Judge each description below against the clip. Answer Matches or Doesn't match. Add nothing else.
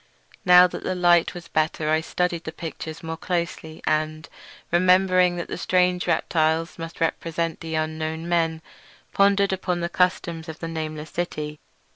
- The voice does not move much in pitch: Matches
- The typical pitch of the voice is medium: Matches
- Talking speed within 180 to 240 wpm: Doesn't match